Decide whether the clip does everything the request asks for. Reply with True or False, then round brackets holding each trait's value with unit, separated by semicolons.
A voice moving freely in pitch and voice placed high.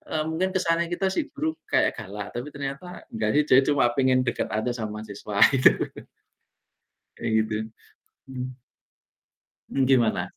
False (6.5 semitones; 130 Hz)